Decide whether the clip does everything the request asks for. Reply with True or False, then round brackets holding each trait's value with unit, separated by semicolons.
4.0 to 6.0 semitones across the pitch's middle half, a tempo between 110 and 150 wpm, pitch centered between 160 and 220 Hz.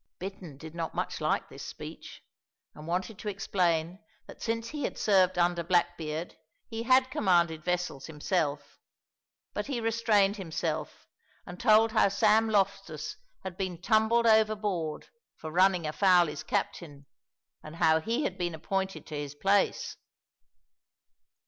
True (4.6 semitones; 140 wpm; 185 Hz)